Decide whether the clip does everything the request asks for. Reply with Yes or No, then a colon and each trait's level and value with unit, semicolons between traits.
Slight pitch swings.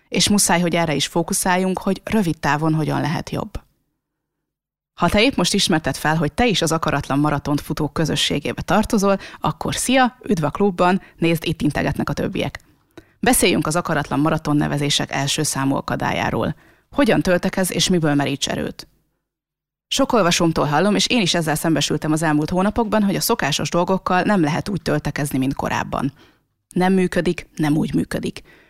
No: average, 4.2 semitones